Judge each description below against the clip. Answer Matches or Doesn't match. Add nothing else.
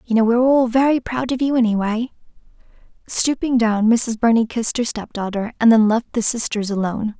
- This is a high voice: Matches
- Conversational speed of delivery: Matches